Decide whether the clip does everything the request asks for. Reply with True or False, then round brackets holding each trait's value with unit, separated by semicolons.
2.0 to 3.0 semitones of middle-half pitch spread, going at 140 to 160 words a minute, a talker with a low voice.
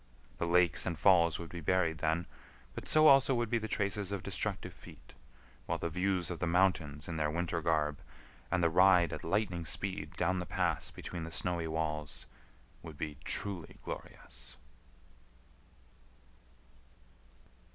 True (2.6 semitones; 150 wpm; 85 Hz)